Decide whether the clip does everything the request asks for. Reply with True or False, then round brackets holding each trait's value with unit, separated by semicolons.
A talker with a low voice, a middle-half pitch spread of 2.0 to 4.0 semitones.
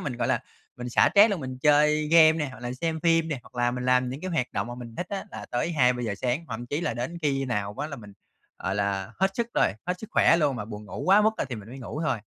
False (130 Hz; 5.0 semitones)